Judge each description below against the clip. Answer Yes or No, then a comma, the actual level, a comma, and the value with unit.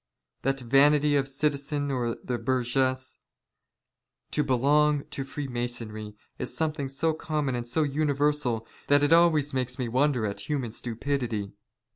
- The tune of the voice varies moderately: Yes, average, 3.3 semitones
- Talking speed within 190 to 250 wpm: No, average, 155 wpm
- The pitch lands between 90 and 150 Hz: Yes, low, 135 Hz